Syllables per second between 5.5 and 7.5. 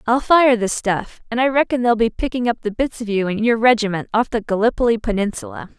Yes: 5.9 syllables/s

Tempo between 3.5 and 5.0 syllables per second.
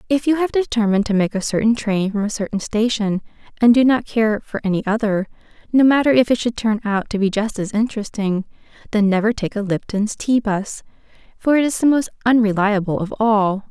No: 5.6 syllables/s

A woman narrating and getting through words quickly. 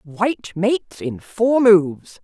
No: female; slow, 135 wpm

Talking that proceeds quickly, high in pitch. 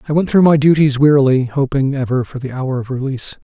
No: fast, 220 wpm; low, 135 Hz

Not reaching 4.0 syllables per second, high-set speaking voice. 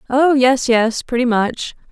Yes: 3.8 syllables/s; very high, 250 Hz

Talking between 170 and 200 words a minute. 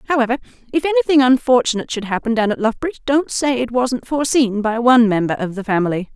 Yes: average, 195 wpm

